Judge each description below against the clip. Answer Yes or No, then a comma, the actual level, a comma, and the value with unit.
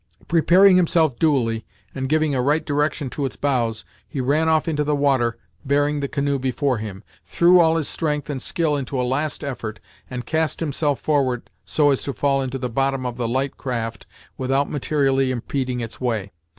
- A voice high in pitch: No, medium, 140 Hz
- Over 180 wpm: Yes, average, 190 wpm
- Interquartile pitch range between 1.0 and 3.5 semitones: Yes, average, 2.9 semitones